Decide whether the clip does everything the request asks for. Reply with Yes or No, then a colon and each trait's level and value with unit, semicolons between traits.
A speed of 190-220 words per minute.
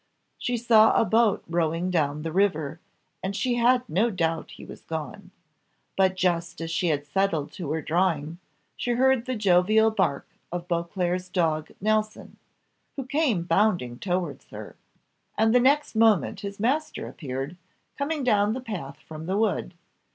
No: average, 160 wpm